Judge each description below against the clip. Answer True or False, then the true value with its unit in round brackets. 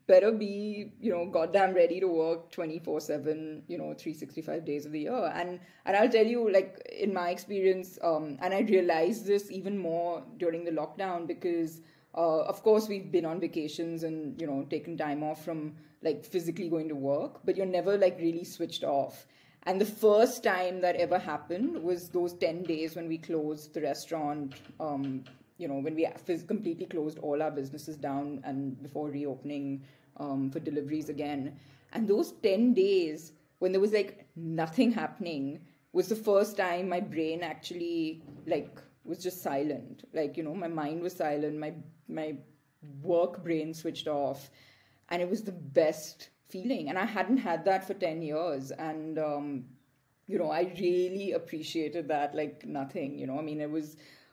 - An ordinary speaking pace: True (180 wpm)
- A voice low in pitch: False (165 Hz)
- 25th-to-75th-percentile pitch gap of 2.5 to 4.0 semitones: True (3.4 semitones)